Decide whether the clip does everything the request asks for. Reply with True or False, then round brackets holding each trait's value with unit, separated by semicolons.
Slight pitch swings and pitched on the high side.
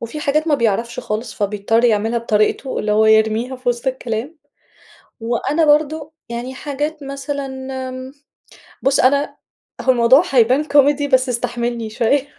False (3.5 semitones; 255 Hz)